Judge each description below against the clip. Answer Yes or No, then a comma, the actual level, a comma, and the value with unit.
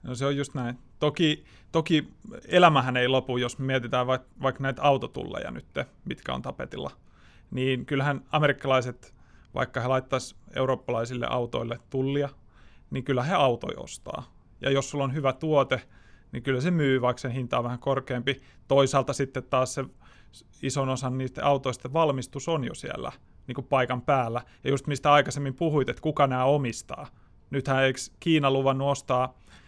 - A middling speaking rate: No, fast, 160 wpm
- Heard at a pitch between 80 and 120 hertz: No, low, 135 Hz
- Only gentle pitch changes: Yes, narrow, 2.0 semitones